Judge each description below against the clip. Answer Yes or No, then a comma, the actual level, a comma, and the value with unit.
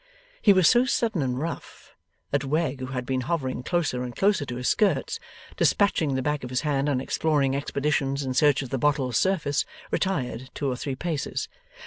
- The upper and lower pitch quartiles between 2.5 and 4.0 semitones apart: Yes, average, 3.7 semitones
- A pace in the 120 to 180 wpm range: No, average, 190 wpm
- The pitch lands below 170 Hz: Yes, medium, 140 Hz